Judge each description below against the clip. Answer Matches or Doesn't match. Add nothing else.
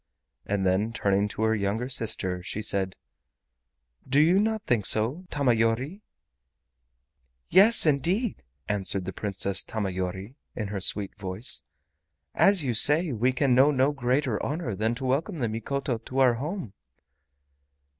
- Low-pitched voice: Matches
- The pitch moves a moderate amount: Doesn't match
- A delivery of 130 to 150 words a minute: Matches